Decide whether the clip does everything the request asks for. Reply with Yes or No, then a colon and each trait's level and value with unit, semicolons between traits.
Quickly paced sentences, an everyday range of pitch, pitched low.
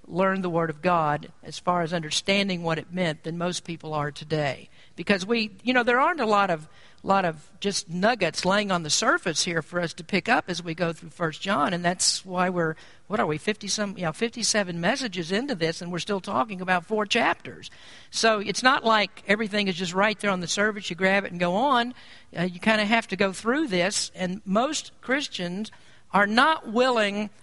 No: fast, 220 wpm; average, 3.6 semitones; high, 190 Hz